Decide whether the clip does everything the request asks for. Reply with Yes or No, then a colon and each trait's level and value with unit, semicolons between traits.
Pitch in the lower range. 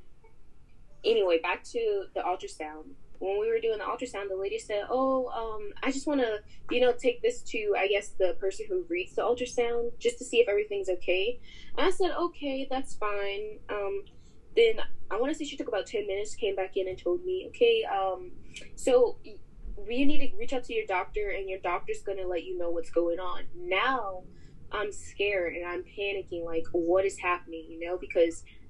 No: high, 210 Hz